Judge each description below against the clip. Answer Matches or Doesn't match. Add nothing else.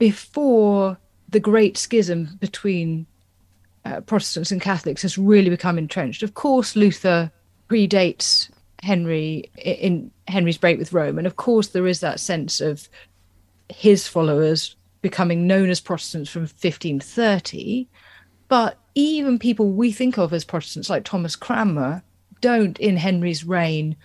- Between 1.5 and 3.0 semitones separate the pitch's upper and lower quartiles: Doesn't match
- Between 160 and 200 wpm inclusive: Doesn't match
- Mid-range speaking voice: Matches